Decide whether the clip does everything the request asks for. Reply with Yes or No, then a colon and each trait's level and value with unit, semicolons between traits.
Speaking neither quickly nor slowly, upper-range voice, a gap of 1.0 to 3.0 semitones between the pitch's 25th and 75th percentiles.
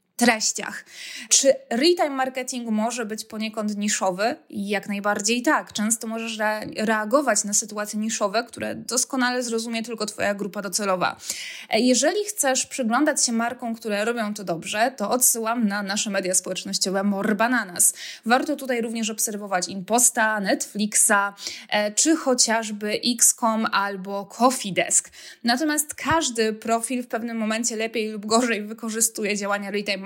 Yes: average, 130 wpm; high, 225 Hz; average, 2.7 semitones